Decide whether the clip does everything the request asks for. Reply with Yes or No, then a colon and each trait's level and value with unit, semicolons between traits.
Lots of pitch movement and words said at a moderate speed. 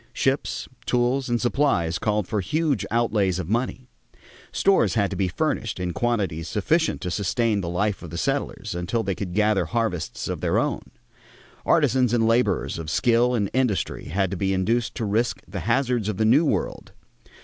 No: average, 4.4 semitones; average, 180 wpm